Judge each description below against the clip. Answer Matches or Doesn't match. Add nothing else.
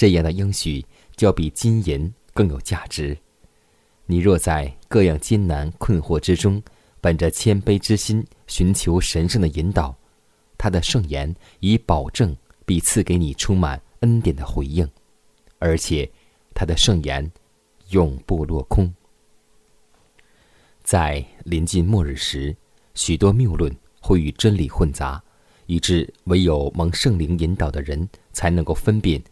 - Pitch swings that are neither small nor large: Matches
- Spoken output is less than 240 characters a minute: Matches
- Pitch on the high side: Doesn't match